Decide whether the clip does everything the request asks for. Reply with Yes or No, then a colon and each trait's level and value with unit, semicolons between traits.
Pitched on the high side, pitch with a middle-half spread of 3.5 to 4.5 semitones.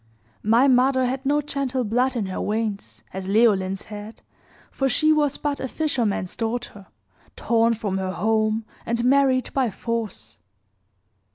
Yes: high, 230 Hz; average, 3.9 semitones